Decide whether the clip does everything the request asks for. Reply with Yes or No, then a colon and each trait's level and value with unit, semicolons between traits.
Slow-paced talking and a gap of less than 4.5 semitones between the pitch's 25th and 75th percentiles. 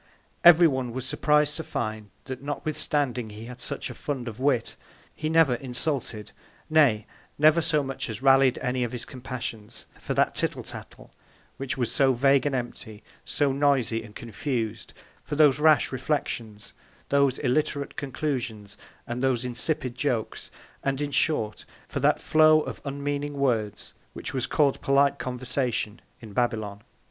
No: average, 155 wpm; average, 3.5 semitones